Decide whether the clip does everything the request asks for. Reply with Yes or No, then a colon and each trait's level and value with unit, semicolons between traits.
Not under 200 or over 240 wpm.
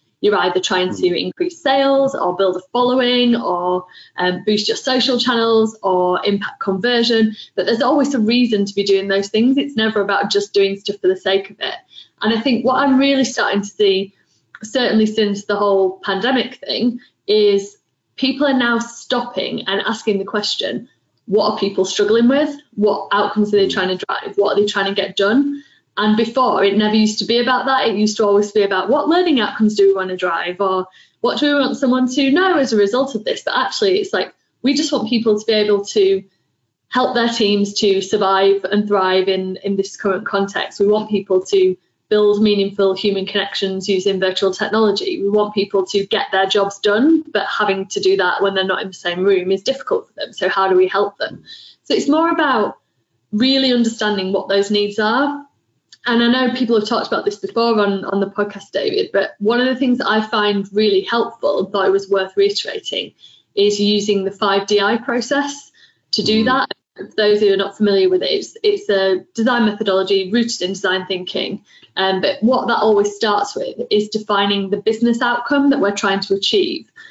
Yes: fast, 205 wpm